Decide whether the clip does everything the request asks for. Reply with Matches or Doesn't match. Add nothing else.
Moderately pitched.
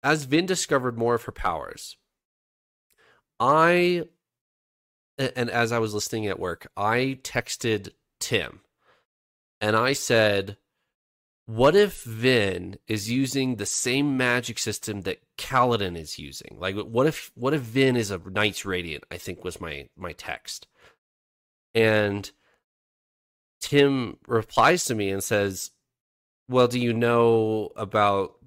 Doesn't match